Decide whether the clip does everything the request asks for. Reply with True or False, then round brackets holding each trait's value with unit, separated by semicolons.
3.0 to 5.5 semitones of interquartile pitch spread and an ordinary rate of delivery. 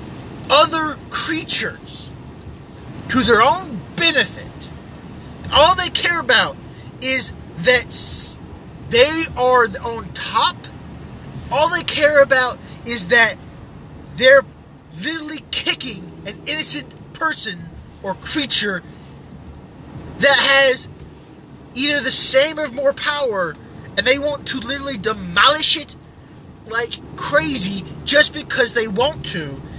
False (3.8 semitones; 105 wpm)